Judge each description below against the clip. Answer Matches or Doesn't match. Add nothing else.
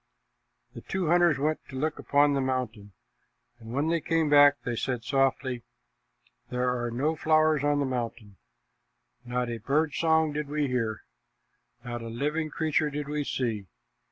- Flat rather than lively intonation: Doesn't match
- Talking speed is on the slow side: Doesn't match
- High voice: Doesn't match